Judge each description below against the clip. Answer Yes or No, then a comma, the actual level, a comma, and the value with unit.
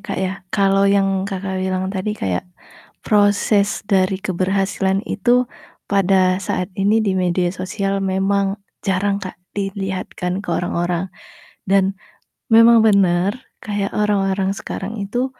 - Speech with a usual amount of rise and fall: No, narrow, 1.3 semitones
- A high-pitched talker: Yes, high, 195 Hz